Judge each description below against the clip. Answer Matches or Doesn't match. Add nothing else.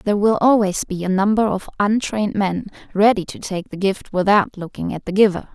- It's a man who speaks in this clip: Doesn't match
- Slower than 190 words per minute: Doesn't match